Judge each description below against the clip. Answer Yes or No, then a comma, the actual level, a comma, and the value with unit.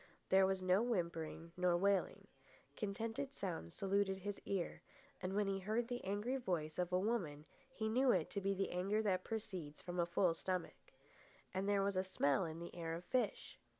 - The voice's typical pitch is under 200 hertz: Yes, high, 190 Hz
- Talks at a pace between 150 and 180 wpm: No, average, 190 wpm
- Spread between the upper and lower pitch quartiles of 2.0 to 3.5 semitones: Yes, average, 2.7 semitones